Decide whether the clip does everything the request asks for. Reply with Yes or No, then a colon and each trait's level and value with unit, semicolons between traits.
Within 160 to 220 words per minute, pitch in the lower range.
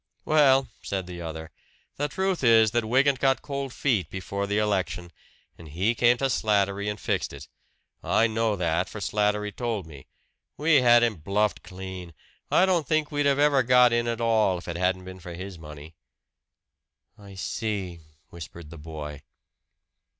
Yes: average, 170 wpm; low, 105 Hz